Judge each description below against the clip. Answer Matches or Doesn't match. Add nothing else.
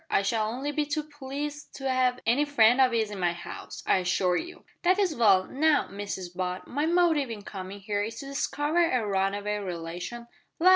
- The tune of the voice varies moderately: Doesn't match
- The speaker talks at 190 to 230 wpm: Matches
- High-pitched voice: Matches